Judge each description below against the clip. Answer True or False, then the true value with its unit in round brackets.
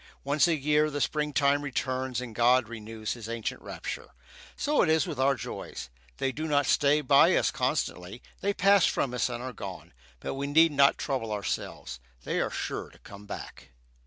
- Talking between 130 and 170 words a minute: False (190 wpm)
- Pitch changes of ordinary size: True (4.2 semitones)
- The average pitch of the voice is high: False (135 Hz)